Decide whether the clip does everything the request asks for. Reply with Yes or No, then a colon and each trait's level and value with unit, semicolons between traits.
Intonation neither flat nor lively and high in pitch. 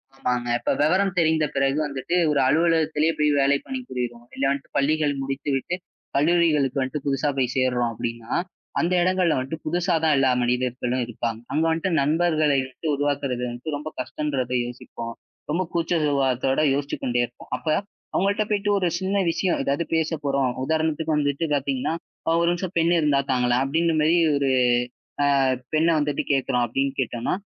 No: average, 3.8 semitones; medium, 145 Hz